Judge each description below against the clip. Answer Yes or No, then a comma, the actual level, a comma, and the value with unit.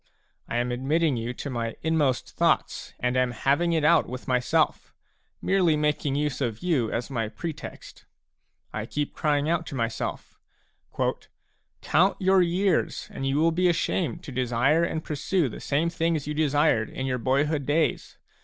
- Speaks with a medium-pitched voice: Yes, medium, 145 Hz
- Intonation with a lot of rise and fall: No, average, 4.4 semitones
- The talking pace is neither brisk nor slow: Yes, average, 165 wpm